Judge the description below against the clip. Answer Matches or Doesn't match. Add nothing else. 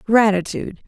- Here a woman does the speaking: Matches